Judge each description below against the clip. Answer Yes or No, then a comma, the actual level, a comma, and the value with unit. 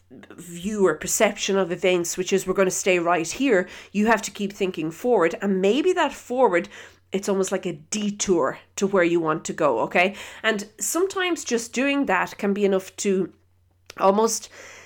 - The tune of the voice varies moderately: Yes, average, 3.7 semitones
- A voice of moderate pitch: No, high, 195 Hz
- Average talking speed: Yes, average, 180 wpm